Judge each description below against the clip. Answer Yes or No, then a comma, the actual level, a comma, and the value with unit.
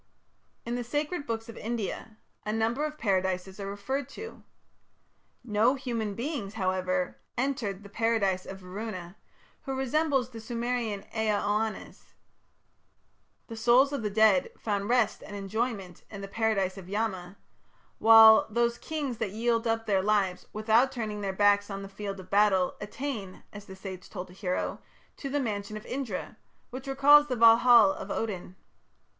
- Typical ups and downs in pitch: Yes, average, 3.3 semitones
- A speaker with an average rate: Yes, average, 160 wpm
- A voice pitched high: Yes, high, 220 Hz